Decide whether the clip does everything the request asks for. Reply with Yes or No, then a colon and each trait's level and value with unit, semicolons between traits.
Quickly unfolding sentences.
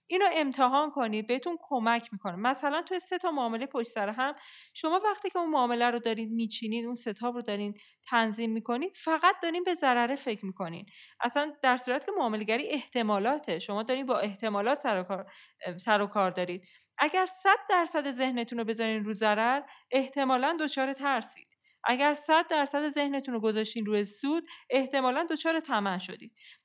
Yes: fast, 160 wpm